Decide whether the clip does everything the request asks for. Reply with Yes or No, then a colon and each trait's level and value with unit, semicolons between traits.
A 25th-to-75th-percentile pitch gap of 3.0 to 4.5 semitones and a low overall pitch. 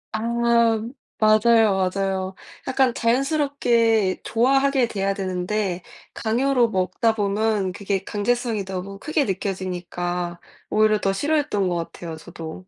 No: average, 3.9 semitones; high, 205 Hz